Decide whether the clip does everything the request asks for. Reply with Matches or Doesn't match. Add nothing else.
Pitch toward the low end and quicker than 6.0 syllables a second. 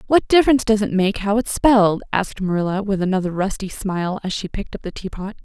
Doesn't match